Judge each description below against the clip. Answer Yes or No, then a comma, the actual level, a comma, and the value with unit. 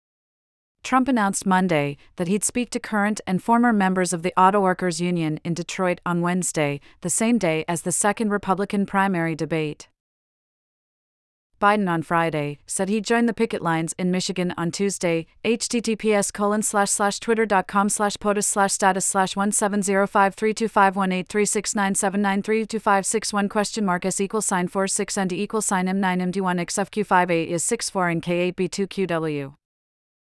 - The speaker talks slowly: No, average, 160 wpm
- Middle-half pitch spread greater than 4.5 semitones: No, average, 2.7 semitones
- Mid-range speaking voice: No, high, 195 Hz